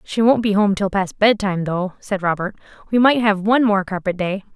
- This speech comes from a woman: Yes, female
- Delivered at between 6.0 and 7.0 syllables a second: No, 5.5 syllables/s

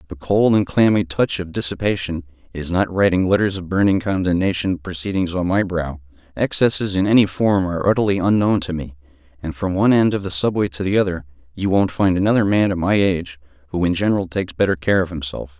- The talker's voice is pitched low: Yes, very low, 90 Hz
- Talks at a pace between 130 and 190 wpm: No, fast, 205 wpm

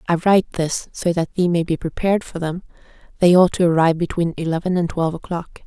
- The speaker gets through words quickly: Yes, fast, 210 wpm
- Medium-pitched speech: Yes, medium, 170 Hz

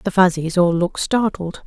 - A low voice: No, medium, 180 Hz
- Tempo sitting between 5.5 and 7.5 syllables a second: No, 5.3 syllables/s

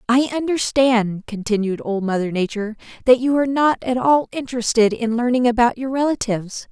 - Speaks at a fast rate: No, average, 160 wpm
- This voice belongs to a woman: Yes, female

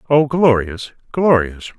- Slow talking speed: Yes, slow, 100 wpm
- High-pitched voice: No, low, 125 Hz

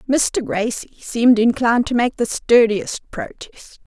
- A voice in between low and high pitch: No, high, 230 Hz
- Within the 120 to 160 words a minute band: Yes, slow, 135 wpm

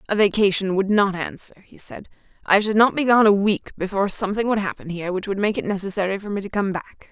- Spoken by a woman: Yes, female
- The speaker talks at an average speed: No, fast, 245 wpm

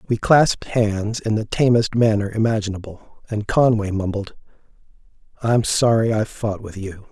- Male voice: Yes, male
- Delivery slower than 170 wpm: Yes, average, 145 wpm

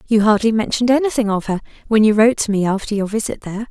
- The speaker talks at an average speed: No, fast, 245 wpm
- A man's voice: No, female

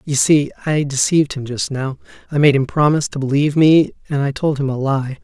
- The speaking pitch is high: No, medium, 140 Hz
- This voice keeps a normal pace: No, fast, 230 wpm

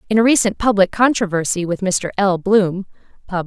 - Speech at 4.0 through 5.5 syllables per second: Yes, 5.4 syllables/s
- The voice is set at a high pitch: Yes, high, 195 Hz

